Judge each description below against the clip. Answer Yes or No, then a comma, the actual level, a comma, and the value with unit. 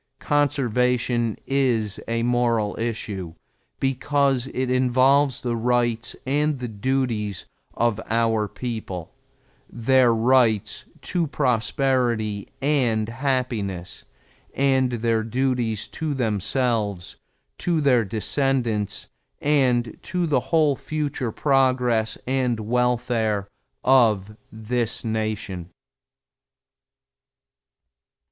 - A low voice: Yes, low, 120 Hz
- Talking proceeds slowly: Yes, slow, 85 wpm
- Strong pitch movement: No, average, 3.2 semitones